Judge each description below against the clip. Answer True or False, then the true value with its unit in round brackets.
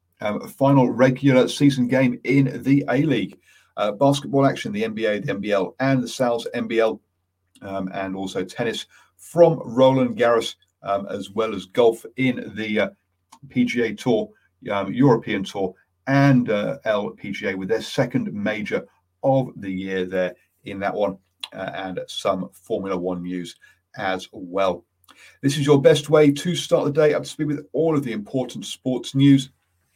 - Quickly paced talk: False (160 wpm)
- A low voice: True (125 Hz)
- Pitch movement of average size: False (6.4 semitones)